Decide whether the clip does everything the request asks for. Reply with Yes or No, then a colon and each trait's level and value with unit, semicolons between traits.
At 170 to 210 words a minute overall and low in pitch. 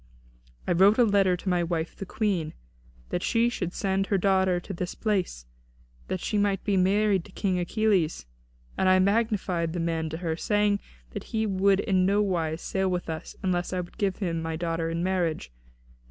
No: average, 195 wpm; medium, 185 Hz